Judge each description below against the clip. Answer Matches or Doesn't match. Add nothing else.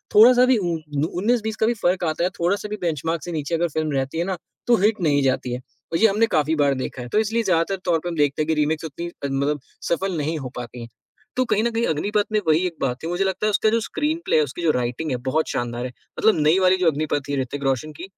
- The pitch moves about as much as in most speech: Doesn't match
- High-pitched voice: Doesn't match